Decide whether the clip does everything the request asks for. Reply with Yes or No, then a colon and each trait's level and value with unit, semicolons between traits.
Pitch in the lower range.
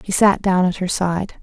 No: medium, 185 Hz